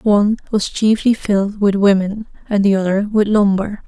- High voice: Yes, high, 205 Hz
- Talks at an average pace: Yes, average, 170 wpm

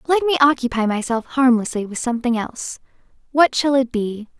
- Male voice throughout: No, female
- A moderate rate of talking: Yes, average, 165 wpm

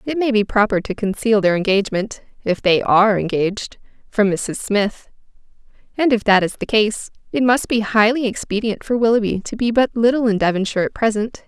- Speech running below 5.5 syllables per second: Yes, 5.2 syllables/s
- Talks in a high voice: Yes, high, 215 Hz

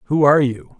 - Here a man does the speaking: Yes, male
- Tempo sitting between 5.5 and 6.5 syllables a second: No, 6.8 syllables/s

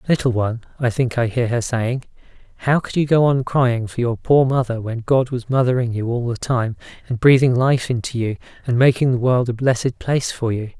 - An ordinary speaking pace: No, fast, 220 wpm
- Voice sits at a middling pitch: No, low, 125 Hz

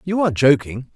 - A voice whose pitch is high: No, medium, 145 Hz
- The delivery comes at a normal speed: Yes, average, 190 wpm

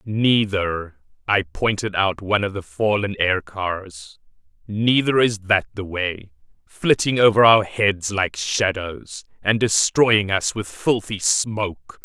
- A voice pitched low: Yes, low, 100 Hz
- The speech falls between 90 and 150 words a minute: Yes, slow, 135 wpm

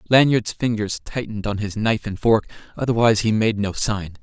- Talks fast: No, average, 185 wpm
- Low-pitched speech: Yes, low, 110 Hz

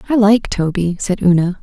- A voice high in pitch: Yes, high, 195 Hz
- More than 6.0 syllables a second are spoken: No, 4.9 syllables/s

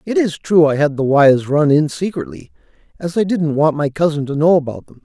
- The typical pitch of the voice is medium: Yes, medium, 160 Hz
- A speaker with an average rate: No, fast, 240 wpm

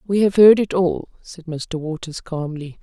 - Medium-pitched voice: Yes, medium, 175 Hz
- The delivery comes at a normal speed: Yes, average, 190 wpm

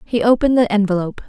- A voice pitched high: Yes, high, 220 Hz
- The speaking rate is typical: Yes, average, 190 wpm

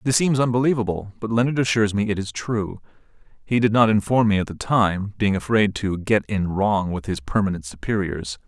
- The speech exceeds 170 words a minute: Yes, average, 200 wpm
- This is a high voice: No, low, 105 Hz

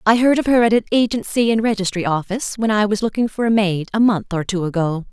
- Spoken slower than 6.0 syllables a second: No, 6.2 syllables/s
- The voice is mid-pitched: No, high, 210 Hz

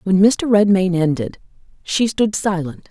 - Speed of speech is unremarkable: Yes, average, 145 wpm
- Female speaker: Yes, female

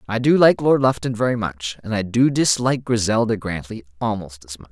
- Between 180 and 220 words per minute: Yes, fast, 205 wpm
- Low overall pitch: Yes, low, 110 Hz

